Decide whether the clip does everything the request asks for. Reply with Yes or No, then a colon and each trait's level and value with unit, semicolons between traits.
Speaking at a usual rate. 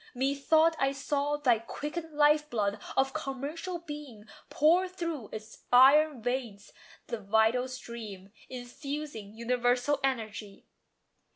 No: slow, 110 wpm